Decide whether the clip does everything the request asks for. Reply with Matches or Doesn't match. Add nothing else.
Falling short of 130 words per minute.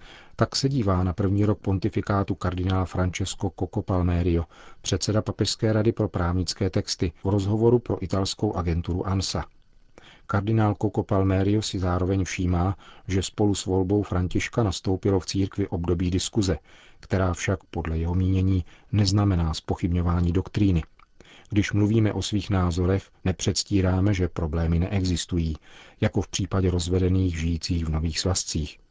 Doesn't match